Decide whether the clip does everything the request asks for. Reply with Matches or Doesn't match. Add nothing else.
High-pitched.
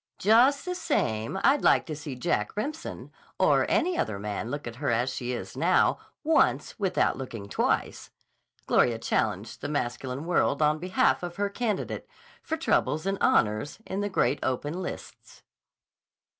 Doesn't match